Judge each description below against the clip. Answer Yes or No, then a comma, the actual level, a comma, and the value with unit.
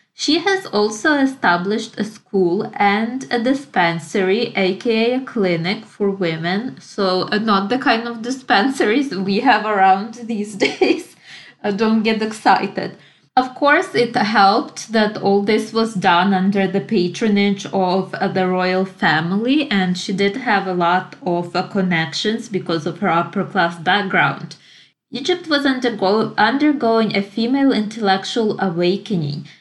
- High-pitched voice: Yes, high, 205 Hz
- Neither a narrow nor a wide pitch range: Yes, average, 4.0 semitones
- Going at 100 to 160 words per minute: Yes, average, 140 wpm